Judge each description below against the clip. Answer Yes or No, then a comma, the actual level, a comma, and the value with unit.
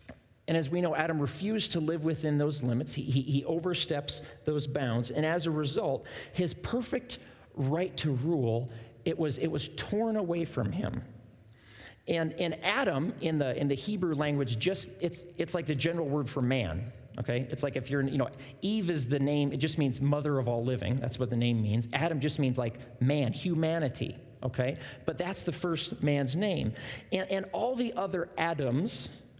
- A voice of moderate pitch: Yes, medium, 145 Hz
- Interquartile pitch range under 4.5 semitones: No, average, 4.8 semitones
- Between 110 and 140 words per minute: No, average, 190 wpm